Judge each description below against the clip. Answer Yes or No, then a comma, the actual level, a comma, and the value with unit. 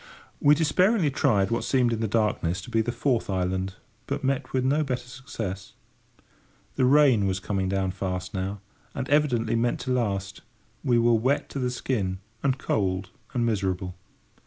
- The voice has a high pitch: No, low, 115 Hz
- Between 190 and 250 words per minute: No, average, 170 wpm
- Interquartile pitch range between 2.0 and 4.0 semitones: No, wide, 5.4 semitones